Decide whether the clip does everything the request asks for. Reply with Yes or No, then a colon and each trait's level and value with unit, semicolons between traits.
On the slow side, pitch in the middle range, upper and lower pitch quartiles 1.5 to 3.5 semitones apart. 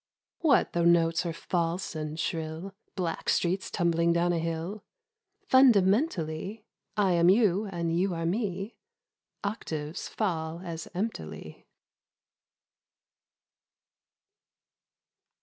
Yes: slow, 100 wpm; medium, 175 Hz; average, 3.1 semitones